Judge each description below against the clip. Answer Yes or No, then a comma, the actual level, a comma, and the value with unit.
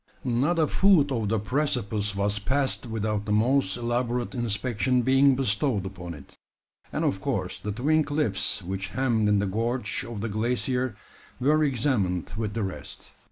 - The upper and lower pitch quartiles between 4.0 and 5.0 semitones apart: Yes, average, 4.3 semitones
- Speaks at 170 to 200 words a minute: No, average, 160 wpm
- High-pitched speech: No, low, 115 Hz